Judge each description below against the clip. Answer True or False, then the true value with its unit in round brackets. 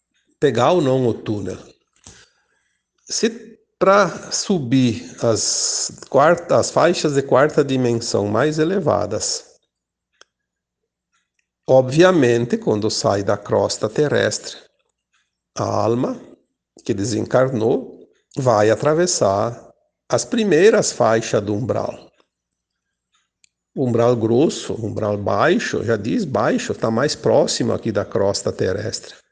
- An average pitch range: False (6.3 semitones)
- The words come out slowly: True (100 wpm)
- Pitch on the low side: True (120 Hz)